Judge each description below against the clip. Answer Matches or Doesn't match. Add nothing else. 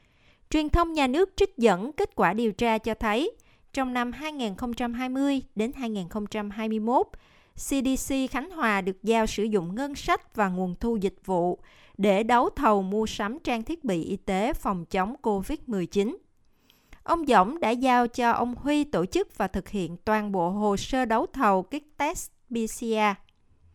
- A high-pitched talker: Matches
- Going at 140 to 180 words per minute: Matches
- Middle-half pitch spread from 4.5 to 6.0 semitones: Matches